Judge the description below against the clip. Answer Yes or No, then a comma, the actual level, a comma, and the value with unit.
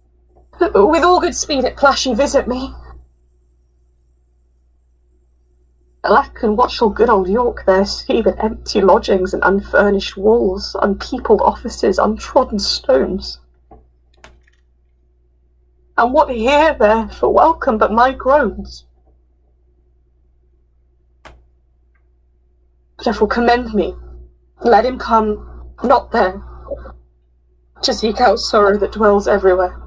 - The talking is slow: Yes, slow, 100 wpm